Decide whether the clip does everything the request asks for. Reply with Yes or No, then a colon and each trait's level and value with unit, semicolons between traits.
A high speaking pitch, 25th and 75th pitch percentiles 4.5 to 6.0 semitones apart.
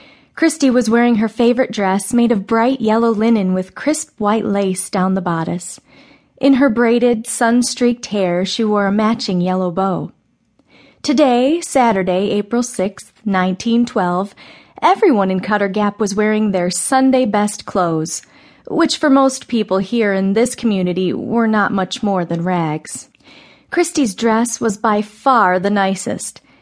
No: high, 215 Hz; average, 4.1 semitones